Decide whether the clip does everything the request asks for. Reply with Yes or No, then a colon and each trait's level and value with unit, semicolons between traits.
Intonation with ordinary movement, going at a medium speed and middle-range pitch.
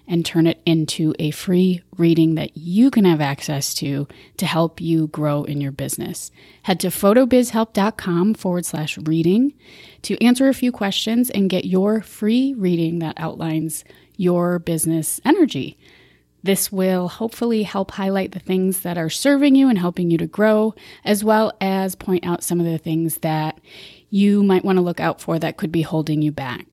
Yes: average, 3.9 semitones; average, 180 wpm; medium, 180 Hz